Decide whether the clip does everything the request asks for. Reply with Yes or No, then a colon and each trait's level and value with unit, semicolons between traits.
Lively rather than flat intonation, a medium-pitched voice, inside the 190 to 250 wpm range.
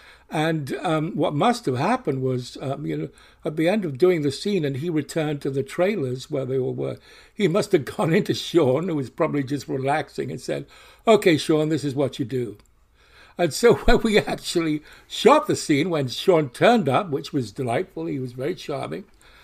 No: average, 4.0 semitones; medium, 150 Hz; fast, 205 wpm